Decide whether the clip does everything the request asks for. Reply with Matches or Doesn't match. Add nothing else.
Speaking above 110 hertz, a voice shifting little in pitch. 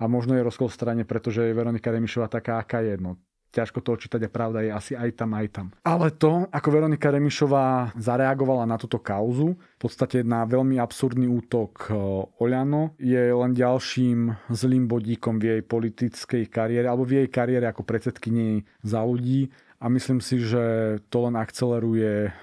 Matches